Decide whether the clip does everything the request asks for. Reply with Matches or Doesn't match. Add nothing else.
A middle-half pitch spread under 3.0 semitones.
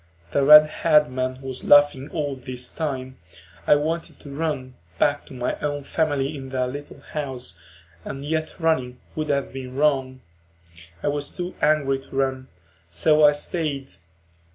Matches